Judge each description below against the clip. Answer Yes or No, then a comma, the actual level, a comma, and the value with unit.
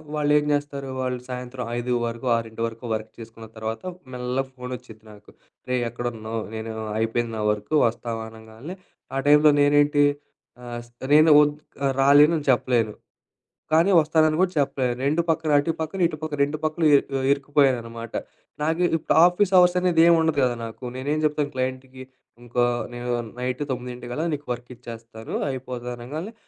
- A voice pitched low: Yes, low, 130 Hz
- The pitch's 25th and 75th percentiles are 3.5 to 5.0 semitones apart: Yes, average, 3.9 semitones